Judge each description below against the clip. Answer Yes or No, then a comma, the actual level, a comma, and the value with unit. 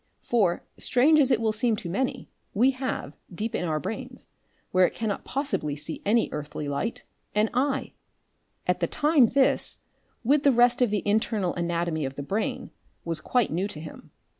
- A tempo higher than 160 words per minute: Yes, average, 180 wpm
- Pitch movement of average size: No, wide, 6.5 semitones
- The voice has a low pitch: No, high, 215 Hz